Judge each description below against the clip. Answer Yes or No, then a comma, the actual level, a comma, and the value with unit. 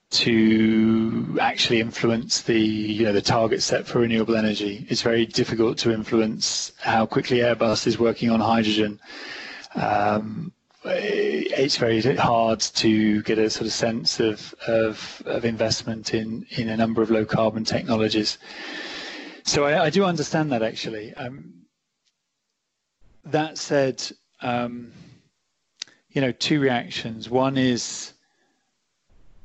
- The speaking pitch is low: Yes, low, 115 Hz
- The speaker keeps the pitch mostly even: No, average, 3.0 semitones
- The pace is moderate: No, slow, 130 wpm